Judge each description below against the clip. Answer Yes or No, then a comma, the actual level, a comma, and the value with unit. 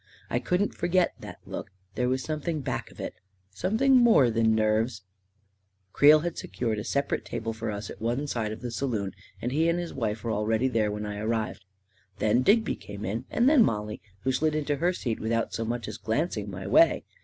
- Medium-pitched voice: No, low, 115 Hz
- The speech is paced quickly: Yes, fast, 210 wpm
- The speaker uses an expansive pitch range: Yes, wide, 6.1 semitones